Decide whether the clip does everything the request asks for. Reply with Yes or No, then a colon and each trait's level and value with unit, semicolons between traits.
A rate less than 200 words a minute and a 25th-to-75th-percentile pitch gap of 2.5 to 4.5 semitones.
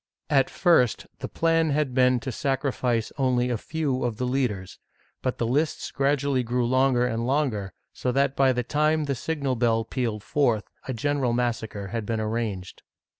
Yes: average, 175 wpm; average, 3.1 semitones